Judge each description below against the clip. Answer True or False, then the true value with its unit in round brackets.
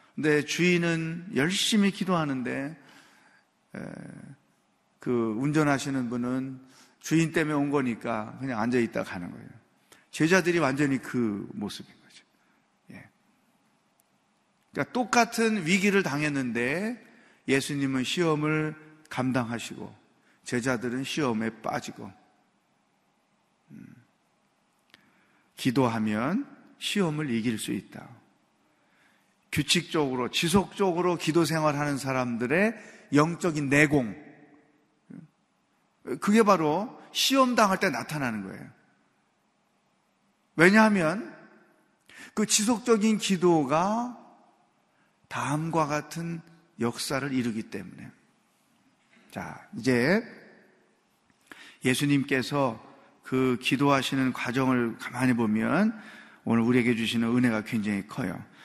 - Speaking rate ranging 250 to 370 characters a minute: False (215 characters per minute)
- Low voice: False (150 Hz)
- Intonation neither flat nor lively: False (6.3 semitones)